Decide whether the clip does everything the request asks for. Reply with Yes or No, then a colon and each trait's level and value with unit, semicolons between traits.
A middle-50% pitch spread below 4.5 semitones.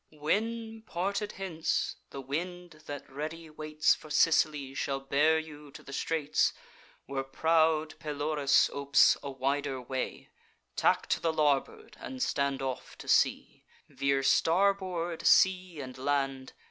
Yes: average, 3.3 semitones